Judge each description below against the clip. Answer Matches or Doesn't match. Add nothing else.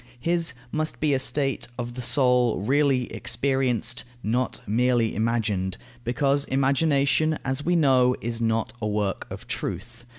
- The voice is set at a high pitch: Doesn't match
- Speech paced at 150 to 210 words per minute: Doesn't match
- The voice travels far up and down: Doesn't match